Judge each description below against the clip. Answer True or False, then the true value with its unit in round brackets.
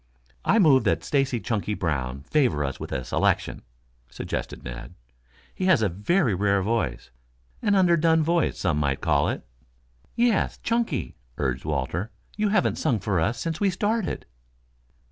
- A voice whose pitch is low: True (115 Hz)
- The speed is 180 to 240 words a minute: False (150 wpm)